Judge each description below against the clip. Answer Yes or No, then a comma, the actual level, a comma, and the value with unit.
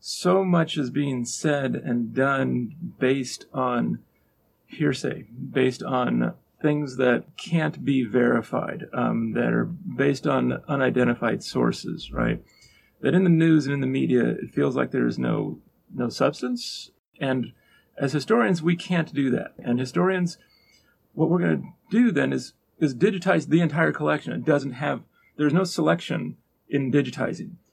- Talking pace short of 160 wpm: Yes, average, 150 wpm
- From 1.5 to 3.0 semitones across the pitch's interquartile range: No, average, 5.3 semitones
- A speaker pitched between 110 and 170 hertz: Yes, medium, 140 Hz